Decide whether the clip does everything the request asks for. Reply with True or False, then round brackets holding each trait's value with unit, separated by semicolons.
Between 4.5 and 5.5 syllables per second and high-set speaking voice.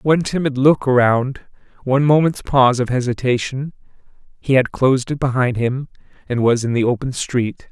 False (5.3 syllables/s; 130 Hz)